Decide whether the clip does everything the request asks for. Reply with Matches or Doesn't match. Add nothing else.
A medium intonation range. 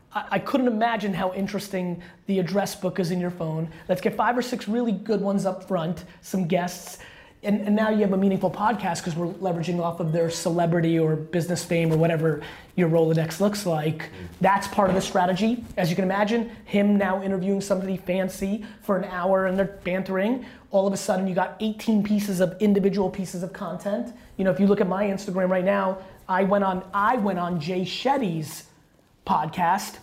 Doesn't match